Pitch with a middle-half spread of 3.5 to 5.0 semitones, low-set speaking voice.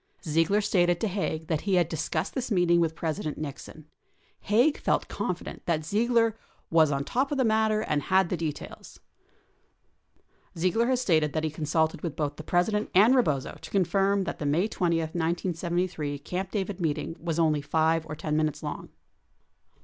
No: average, 4.2 semitones; medium, 170 Hz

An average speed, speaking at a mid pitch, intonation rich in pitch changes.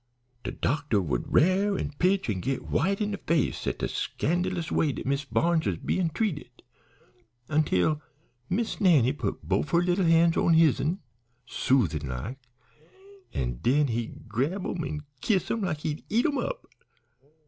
Yes: average, 160 wpm; medium, 160 Hz; wide, 5.7 semitones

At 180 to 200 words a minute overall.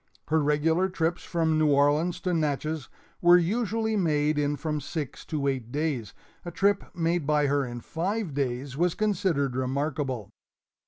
No: average, 155 wpm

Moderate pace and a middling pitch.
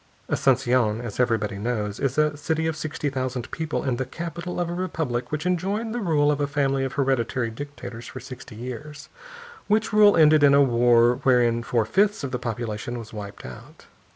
No: average, 190 wpm; low, 130 Hz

